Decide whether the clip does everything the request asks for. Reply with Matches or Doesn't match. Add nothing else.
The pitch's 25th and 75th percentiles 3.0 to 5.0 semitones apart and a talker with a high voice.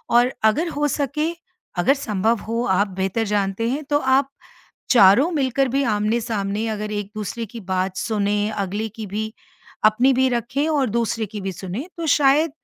Matches